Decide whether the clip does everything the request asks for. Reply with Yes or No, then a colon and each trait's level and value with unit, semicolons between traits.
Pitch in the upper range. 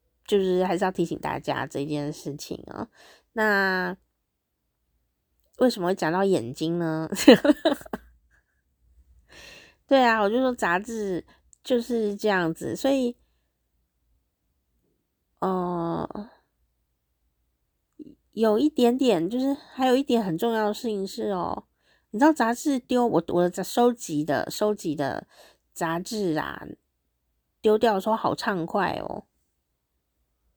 No: medium, 180 Hz